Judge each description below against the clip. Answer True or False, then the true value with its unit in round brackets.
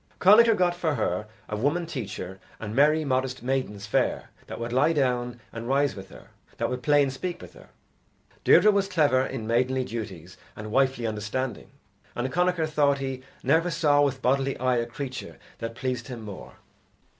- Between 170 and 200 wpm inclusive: True (180 wpm)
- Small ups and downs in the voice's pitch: False (3.9 semitones)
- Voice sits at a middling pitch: False (130 Hz)